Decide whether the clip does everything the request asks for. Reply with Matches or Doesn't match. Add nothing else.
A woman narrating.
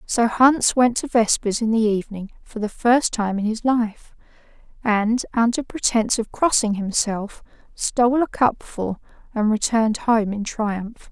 Matches